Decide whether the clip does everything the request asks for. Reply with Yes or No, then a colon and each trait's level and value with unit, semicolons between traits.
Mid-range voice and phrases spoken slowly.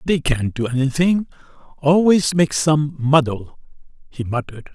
Yes: medium, 145 Hz; slow, 125 wpm